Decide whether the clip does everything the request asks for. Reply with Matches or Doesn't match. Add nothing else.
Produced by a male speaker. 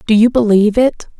Doesn't match